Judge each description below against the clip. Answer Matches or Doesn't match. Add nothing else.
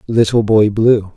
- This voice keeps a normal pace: Matches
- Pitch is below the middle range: Matches